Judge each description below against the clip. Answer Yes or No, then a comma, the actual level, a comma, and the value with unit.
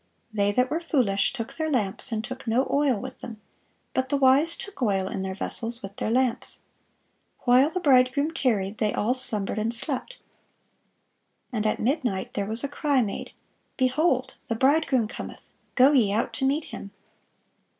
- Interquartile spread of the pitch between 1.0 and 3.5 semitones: No, average, 4.4 semitones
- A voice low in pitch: No, very high, 250 Hz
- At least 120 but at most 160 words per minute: No, average, 170 wpm